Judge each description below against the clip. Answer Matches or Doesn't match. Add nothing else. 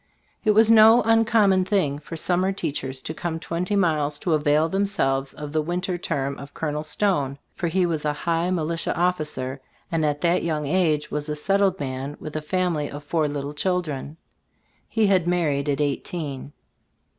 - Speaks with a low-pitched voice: Doesn't match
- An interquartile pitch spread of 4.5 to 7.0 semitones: Doesn't match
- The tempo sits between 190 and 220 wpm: Doesn't match